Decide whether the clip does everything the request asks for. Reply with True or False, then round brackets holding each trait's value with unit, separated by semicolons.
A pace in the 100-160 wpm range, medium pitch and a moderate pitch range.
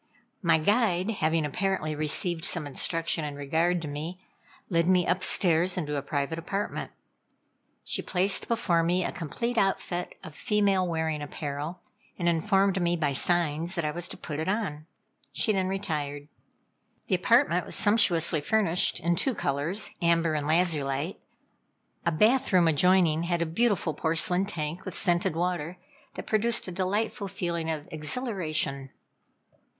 True (150 wpm; 170 Hz; 3.4 semitones)